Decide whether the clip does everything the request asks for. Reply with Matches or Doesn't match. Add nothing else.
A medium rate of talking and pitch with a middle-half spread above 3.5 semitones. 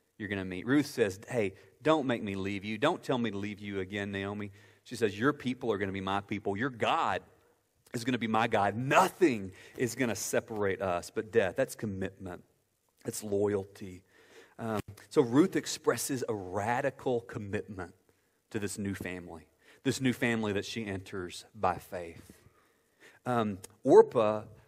Doesn't match